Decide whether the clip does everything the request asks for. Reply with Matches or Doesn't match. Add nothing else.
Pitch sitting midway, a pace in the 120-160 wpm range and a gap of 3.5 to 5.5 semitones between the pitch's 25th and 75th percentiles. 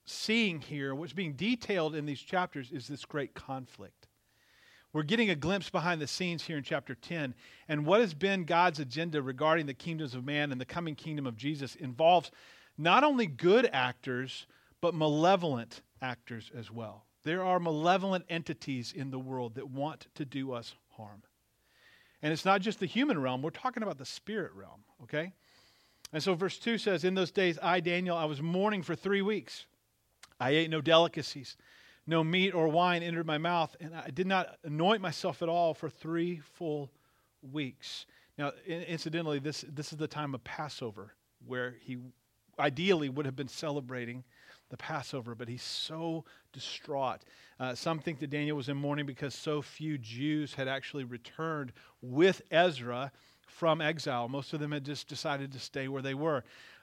Doesn't match